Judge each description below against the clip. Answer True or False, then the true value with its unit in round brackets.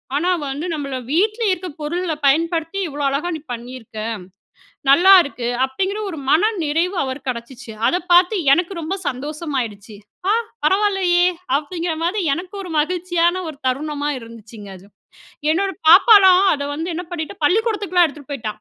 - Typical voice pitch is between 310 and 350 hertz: True (330 Hz)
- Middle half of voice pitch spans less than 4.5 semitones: False (4.8 semitones)